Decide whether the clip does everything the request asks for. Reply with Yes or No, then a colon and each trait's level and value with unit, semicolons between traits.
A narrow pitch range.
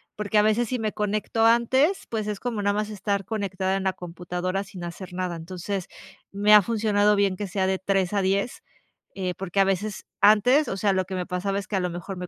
Yes: narrow, 2.1 semitones